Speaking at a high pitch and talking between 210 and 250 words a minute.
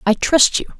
Yes: very high, 255 Hz; fast, 230 wpm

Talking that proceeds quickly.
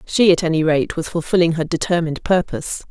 No: average, 185 wpm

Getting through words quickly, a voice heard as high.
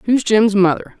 No: average, 180 wpm; high, 205 Hz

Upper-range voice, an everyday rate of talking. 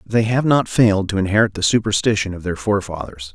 No: low, 105 Hz; average, 195 wpm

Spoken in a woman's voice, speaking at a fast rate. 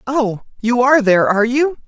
No: female; average, 190 wpm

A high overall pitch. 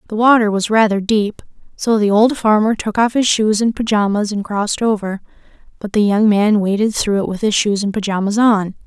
Yes: high, 210 Hz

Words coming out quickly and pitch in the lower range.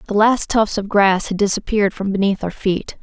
No: fast, 220 wpm; high, 200 Hz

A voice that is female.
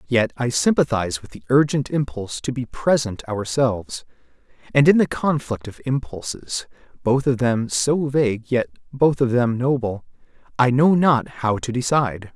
No: male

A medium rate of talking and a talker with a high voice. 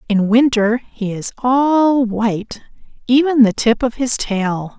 Yes: average, 150 wpm; high, 235 Hz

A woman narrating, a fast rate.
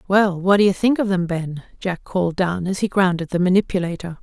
Yes: female; fast, 225 wpm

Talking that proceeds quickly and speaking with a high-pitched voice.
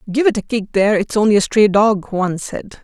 Yes: fast, 210 wpm; high, 210 Hz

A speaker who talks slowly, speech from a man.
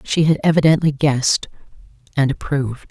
No: slow, 125 wpm; female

